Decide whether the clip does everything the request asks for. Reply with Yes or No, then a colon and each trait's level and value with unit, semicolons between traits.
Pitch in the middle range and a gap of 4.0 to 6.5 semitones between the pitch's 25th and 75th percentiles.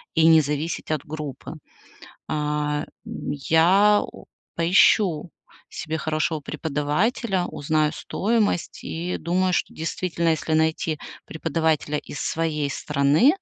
No: medium, 160 Hz; narrow, 2.6 semitones